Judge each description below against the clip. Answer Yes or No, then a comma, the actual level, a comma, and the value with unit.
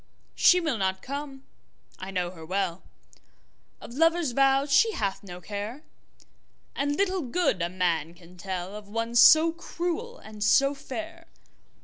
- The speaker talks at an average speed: No, slow, 130 wpm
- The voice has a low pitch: No, high, 230 Hz